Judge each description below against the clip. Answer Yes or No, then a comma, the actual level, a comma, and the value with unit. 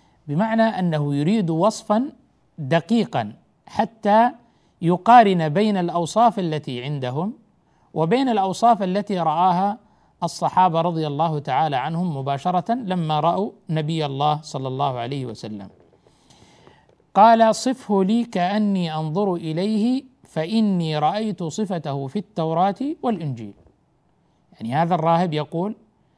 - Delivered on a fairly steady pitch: No, wide, 5.5 semitones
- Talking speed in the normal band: Yes, average, 105 wpm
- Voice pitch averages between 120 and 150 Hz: No, medium, 180 Hz